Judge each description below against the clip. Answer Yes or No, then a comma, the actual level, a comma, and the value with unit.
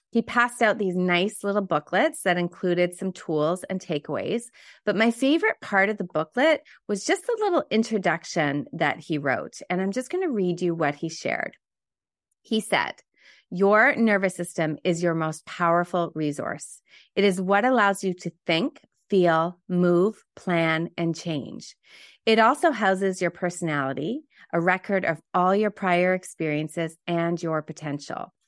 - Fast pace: No, average, 160 wpm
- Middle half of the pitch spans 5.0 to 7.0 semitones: No, average, 4.2 semitones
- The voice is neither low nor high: Yes, medium, 180 Hz